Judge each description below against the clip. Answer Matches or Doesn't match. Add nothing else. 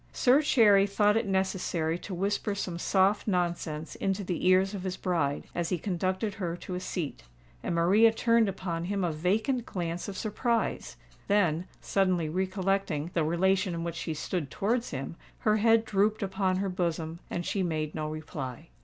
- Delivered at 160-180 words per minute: Matches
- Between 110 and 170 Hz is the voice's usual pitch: Doesn't match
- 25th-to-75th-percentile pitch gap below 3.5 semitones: Matches